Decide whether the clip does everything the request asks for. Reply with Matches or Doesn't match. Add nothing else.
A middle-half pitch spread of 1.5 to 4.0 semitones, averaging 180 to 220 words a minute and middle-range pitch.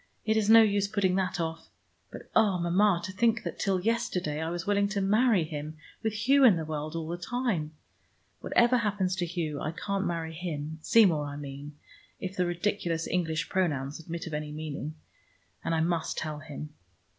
Doesn't match